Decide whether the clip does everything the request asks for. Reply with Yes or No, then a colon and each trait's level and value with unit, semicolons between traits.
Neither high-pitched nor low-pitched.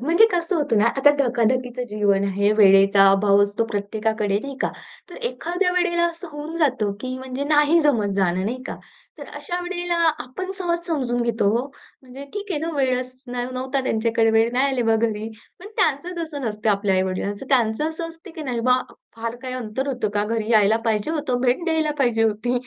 No: very high, 250 Hz